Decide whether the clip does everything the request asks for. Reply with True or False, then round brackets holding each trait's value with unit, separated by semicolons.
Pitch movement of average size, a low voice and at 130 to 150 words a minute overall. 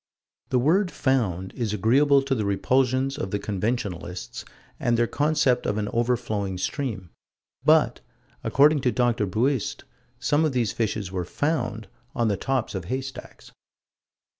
True (4.7 semitones; 120 Hz; 140 wpm)